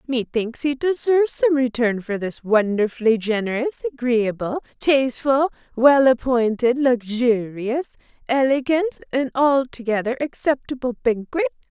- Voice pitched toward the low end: No, very high, 250 Hz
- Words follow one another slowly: Yes, slow, 95 wpm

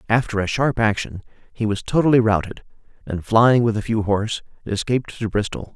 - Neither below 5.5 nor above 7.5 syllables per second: Yes, 5.6 syllables/s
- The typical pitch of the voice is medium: No, low, 110 Hz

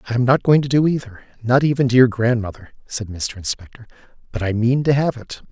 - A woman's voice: No, male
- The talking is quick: Yes, fast, 230 wpm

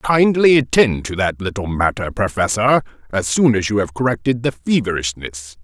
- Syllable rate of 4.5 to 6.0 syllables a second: Yes, 5.0 syllables/s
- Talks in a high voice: No, low, 110 Hz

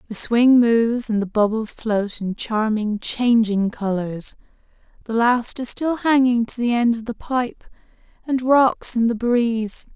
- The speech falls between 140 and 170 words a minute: Yes, average, 165 wpm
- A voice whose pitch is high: Yes, high, 230 Hz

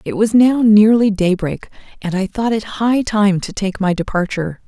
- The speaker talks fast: No, average, 195 wpm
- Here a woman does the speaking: Yes, female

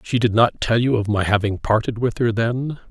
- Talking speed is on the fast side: Yes, fast, 250 wpm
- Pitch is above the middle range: No, low, 115 Hz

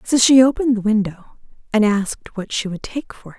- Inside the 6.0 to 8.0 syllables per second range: Yes, 6.1 syllables/s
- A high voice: Yes, high, 225 Hz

